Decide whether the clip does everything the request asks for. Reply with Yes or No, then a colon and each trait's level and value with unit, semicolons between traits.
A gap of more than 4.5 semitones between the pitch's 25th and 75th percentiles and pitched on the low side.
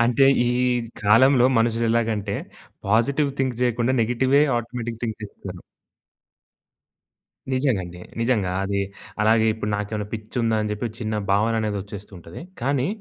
No: average, 2.8 semitones; low, 115 Hz